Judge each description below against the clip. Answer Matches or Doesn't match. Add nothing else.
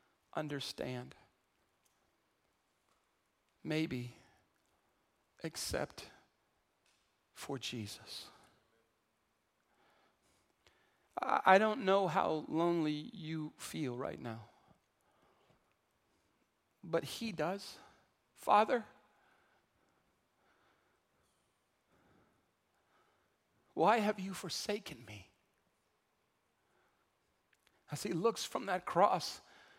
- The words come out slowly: Matches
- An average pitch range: Doesn't match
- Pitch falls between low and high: Matches